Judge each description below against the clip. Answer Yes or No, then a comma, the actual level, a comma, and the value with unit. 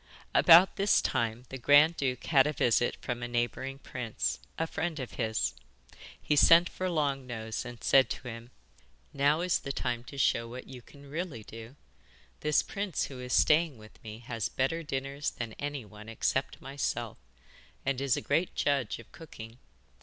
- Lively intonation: No, average, 3.7 semitones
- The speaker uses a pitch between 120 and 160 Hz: Yes, low, 135 Hz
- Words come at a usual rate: Yes, average, 175 wpm